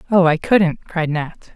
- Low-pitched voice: No, medium, 170 Hz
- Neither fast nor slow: Yes, average, 195 wpm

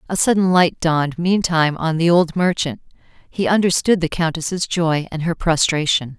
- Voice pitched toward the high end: No, medium, 165 Hz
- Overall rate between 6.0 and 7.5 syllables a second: No, 4.9 syllables/s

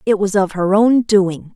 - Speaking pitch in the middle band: No, high, 200 Hz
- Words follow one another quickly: Yes, fast, 230 wpm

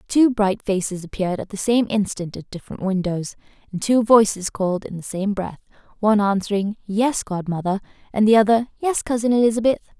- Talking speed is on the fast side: No, average, 175 wpm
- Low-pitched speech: No, high, 205 Hz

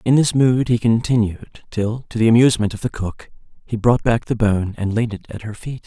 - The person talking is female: No, male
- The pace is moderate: No, fast, 235 wpm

